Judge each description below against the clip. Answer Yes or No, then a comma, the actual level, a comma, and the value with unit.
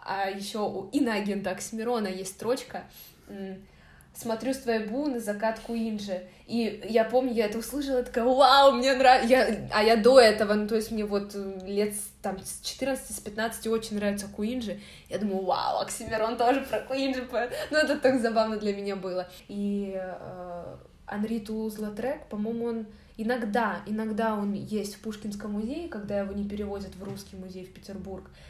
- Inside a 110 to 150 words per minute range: No, fast, 160 wpm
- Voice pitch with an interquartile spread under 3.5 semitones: Yes, average, 3.0 semitones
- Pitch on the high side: Yes, high, 220 Hz